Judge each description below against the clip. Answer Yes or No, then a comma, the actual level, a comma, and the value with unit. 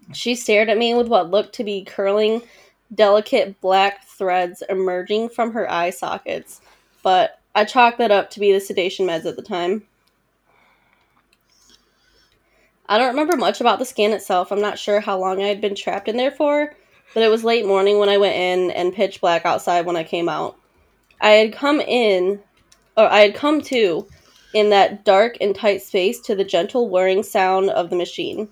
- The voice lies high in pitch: Yes, high, 205 Hz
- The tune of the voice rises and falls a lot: No, average, 3.2 semitones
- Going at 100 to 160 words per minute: No, average, 190 wpm